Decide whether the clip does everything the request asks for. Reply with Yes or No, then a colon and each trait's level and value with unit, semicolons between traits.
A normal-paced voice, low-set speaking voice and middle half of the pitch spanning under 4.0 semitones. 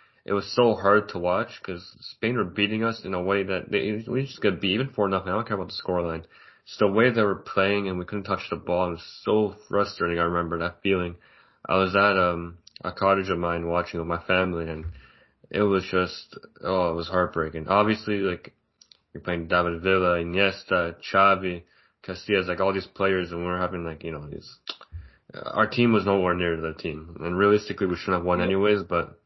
No: fast, 220 wpm; very low, 95 Hz; average, 2.8 semitones